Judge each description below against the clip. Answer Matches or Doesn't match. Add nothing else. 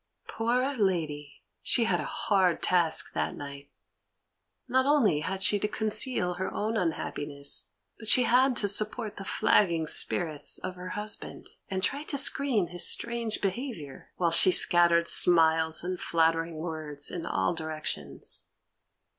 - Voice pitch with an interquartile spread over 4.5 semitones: Matches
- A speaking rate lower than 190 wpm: Matches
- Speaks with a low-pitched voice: Doesn't match